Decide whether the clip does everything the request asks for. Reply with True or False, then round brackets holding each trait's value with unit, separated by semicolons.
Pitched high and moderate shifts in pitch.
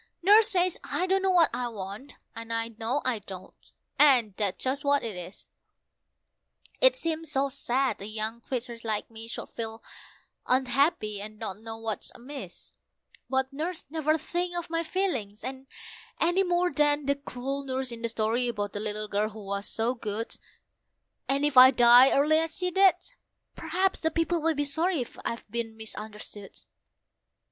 False (255 Hz; 6.2 semitones)